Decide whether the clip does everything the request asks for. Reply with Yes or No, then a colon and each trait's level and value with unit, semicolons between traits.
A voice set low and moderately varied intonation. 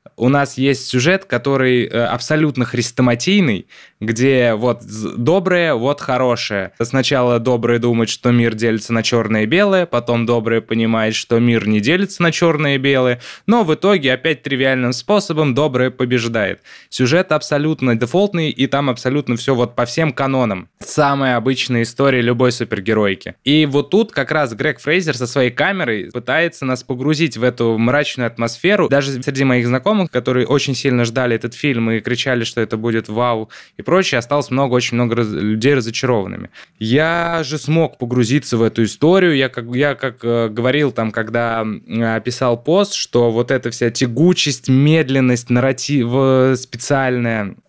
Yes: low, 125 Hz; average, 3.4 semitones